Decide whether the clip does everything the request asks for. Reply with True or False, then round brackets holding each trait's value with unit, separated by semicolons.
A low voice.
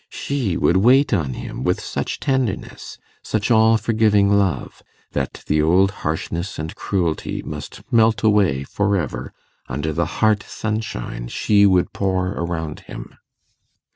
True (95 Hz)